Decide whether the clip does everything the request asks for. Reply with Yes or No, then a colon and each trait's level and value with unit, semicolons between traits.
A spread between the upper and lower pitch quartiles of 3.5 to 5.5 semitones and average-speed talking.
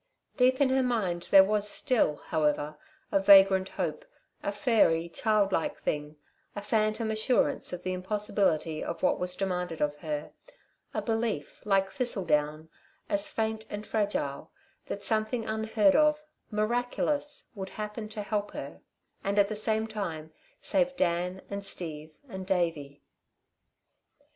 Yes: average, 4.3 semitones; average, 145 wpm